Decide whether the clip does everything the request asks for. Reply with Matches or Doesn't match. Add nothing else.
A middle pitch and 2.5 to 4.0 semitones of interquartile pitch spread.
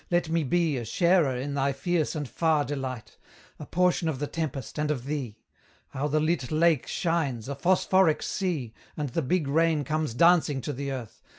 Matches